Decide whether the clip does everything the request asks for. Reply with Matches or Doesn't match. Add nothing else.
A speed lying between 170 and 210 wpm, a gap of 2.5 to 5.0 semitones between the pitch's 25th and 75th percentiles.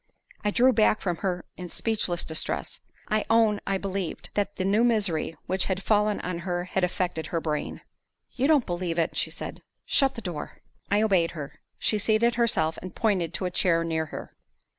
Matches